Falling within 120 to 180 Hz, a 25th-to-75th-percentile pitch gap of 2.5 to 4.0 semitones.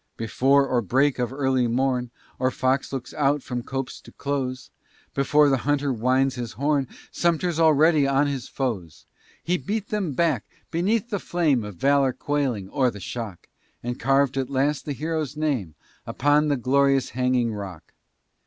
Yes: low, 135 Hz; average, 2.9 semitones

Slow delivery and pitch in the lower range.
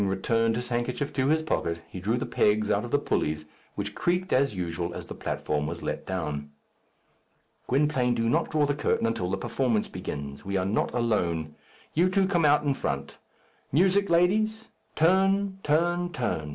No: average, 180 wpm; low, 120 Hz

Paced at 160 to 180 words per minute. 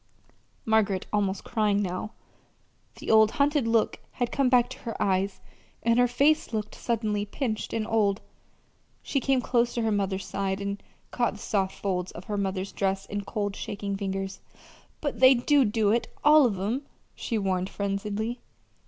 Yes: average, 170 wpm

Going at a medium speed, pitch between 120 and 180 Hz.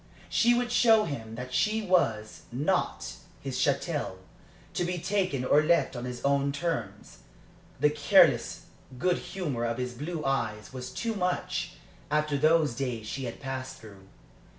Yes: average, 150 wpm; medium, 140 Hz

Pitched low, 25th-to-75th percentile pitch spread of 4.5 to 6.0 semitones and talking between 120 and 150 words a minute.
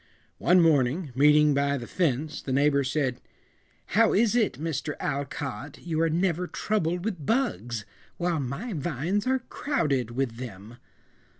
No: medium, 150 Hz; average, 4.9 semitones; average, 140 wpm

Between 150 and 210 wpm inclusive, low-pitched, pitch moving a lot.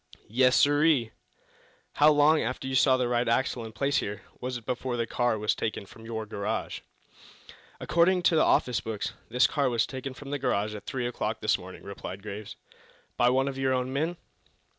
No: average, 195 wpm; low, 125 Hz; average, 3.7 semitones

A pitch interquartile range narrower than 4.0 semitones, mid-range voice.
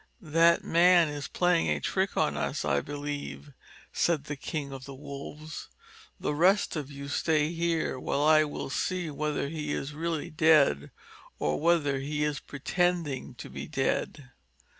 Yes: average, 2.8 semitones; medium, 150 Hz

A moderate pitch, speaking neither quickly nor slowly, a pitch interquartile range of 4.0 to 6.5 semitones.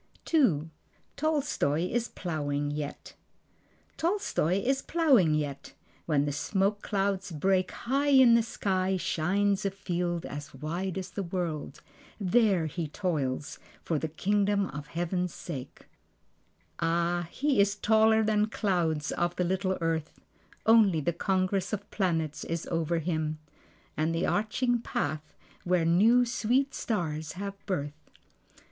No: medium, 180 Hz; slow, 130 wpm; average, 4.7 semitones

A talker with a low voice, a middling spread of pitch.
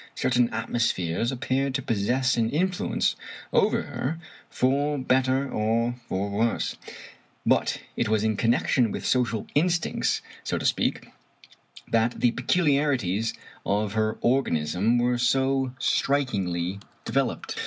Yes: low, 120 Hz; average, 3.5 semitones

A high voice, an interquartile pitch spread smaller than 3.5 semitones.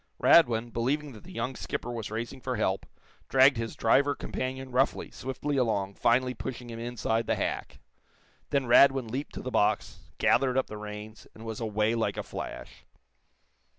No: low, 120 Hz; average, 2.8 semitones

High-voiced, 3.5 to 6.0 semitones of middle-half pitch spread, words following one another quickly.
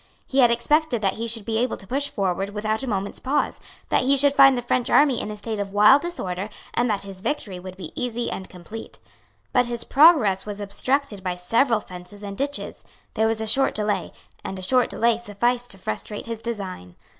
Yes: high, 220 Hz; average, 4.1 semitones; fast, 215 wpm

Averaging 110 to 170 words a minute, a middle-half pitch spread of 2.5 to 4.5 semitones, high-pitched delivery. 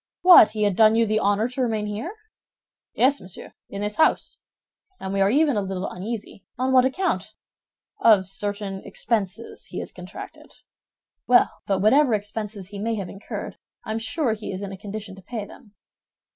No: average, 185 wpm; average, 2.8 semitones; high, 215 Hz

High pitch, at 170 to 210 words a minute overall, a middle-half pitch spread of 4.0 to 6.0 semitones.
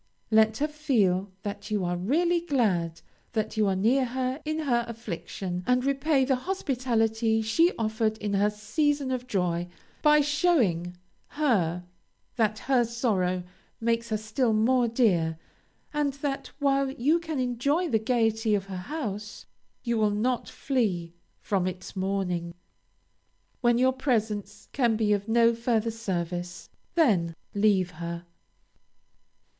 No: high, 225 Hz; average, 140 wpm; average, 4.8 semitones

